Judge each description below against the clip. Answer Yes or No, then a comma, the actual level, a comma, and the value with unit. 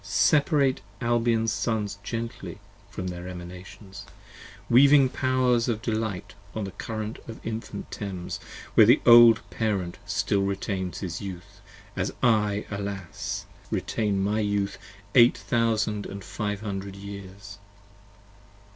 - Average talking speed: No, slow, 120 wpm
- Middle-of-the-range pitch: No, low, 105 Hz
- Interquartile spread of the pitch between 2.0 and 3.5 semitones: Yes, average, 2.7 semitones